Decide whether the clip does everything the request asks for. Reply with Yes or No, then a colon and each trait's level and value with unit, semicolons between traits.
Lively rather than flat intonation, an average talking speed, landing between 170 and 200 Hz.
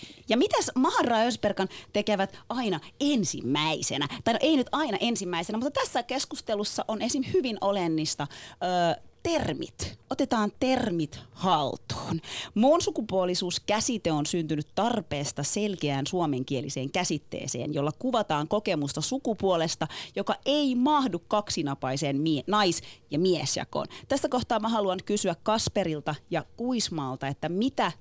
Yes: wide, 7.4 semitones; average, 120 wpm; high, 190 Hz